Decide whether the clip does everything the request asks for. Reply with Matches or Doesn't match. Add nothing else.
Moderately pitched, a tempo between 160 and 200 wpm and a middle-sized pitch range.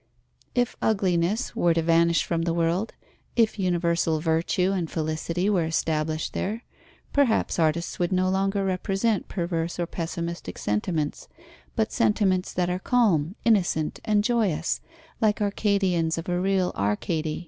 Doesn't match